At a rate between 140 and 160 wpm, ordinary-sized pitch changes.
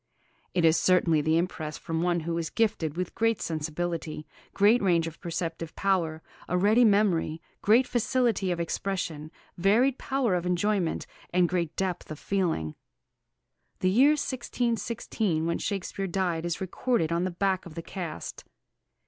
Yes: average, 150 wpm; average, 3.6 semitones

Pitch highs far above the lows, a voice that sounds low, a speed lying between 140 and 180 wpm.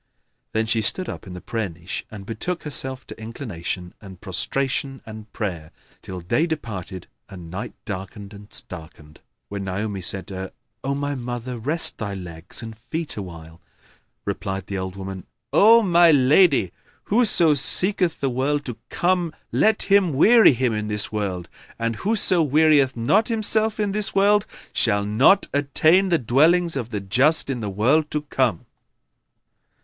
Yes: wide, 8.4 semitones; low, 120 Hz; average, 160 wpm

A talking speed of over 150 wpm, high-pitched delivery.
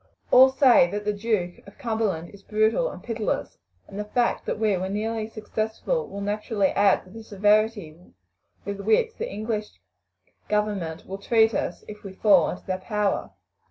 Yes: average, 170 wpm; high, 210 Hz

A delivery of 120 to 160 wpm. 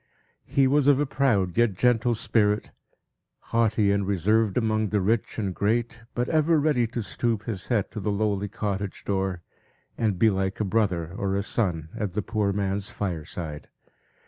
No: average, 170 wpm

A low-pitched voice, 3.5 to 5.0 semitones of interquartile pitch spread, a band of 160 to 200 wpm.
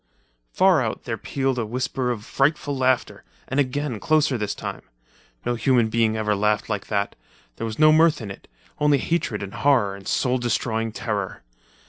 Yes: low, 120 Hz; average, 4.4 semitones; average, 170 wpm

